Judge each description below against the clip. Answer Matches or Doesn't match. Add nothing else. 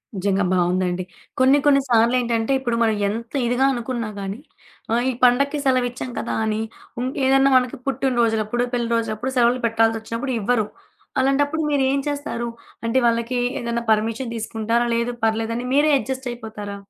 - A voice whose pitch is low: Doesn't match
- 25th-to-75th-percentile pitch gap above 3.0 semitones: Doesn't match